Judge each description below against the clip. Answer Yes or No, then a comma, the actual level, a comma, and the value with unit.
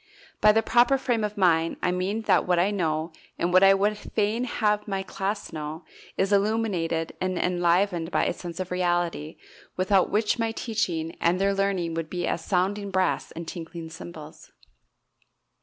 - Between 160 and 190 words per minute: Yes, average, 175 wpm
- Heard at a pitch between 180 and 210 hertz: Yes, medium, 185 Hz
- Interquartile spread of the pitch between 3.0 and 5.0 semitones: Yes, average, 3.4 semitones